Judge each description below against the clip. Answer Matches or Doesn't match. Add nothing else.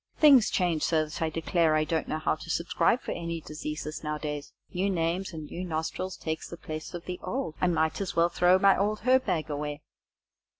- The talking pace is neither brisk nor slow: Doesn't match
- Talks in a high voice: Doesn't match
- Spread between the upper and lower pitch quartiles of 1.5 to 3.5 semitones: Matches